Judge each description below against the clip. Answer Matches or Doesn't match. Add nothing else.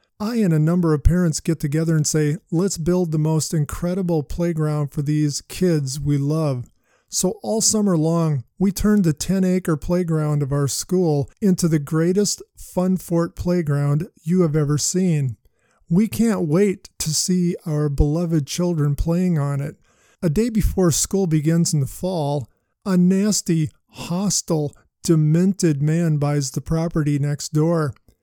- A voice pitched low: Doesn't match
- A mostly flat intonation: Doesn't match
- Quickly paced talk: Doesn't match